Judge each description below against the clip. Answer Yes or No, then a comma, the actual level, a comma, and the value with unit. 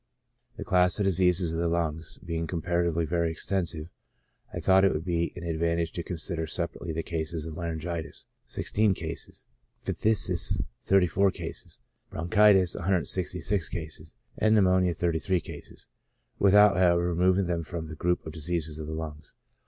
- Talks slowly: No, average, 145 wpm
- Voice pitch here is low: Yes, very low, 85 Hz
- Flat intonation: Yes, narrow, 2.1 semitones